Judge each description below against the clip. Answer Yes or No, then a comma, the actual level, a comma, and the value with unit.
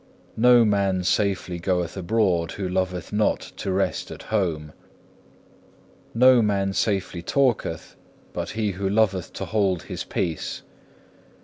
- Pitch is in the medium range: No, very low, 95 Hz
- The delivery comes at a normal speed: No, slow, 125 wpm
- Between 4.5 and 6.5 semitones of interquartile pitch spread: No, average, 2.8 semitones